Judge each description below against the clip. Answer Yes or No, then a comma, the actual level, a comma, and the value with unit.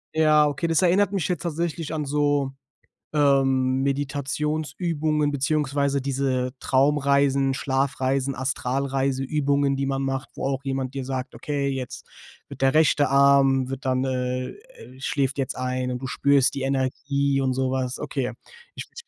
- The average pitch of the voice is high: No, low, 135 Hz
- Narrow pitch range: Yes, narrow, 1.6 semitones